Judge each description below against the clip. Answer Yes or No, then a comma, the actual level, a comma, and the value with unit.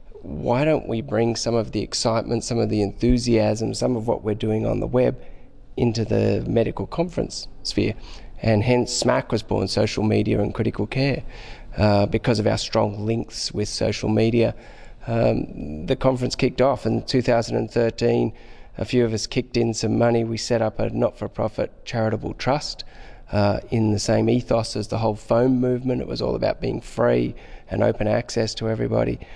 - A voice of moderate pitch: No, low, 115 Hz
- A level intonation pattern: Yes, narrow, 2.0 semitones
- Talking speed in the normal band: Yes, average, 190 wpm